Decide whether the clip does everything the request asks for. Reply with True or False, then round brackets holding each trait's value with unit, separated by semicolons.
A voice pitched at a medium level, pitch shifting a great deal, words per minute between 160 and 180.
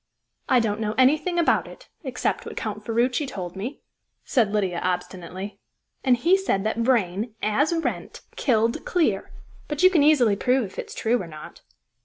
False (230 Hz; 5.7 semitones; 170 wpm)